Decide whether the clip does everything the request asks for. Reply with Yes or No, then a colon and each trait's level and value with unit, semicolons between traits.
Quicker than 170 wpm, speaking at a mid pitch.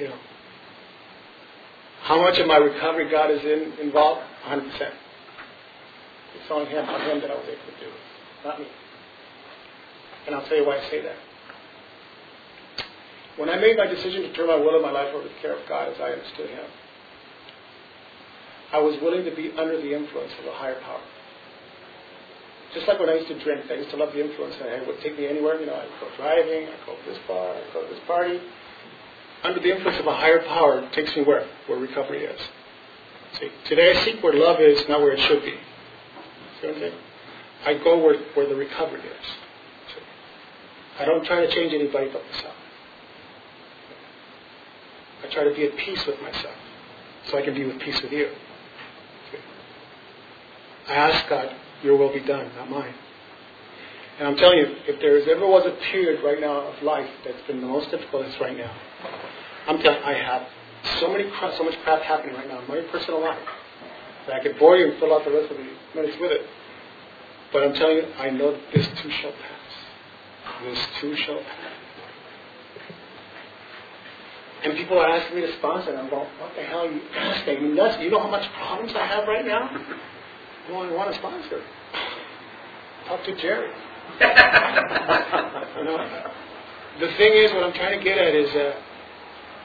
Yes: average, 195 wpm; medium, 160 Hz